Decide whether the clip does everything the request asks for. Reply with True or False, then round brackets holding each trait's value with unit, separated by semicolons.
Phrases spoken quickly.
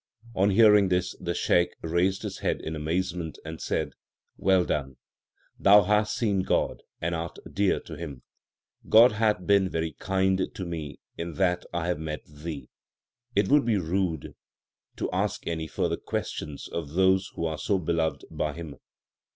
False (165 wpm)